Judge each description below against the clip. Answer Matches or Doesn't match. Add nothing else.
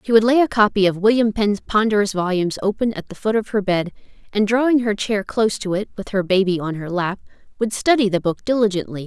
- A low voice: Doesn't match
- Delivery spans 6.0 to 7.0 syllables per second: Matches